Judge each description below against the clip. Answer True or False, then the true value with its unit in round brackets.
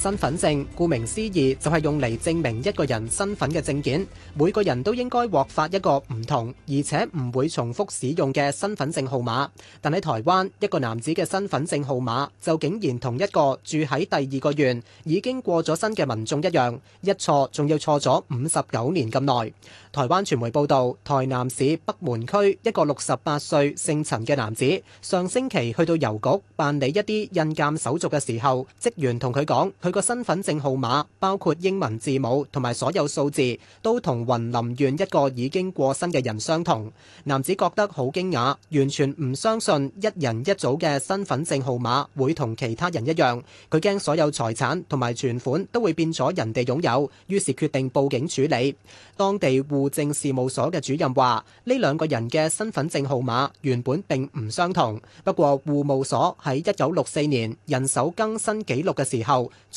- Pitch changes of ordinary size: True (4.5 semitones)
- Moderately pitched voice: True (145 Hz)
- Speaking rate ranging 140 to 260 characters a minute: False (280 characters per minute)